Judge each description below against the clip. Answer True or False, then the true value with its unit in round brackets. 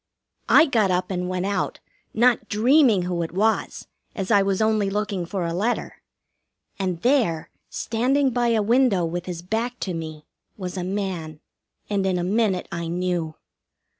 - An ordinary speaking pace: True (165 wpm)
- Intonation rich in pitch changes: False (3.8 semitones)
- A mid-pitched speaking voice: False (195 Hz)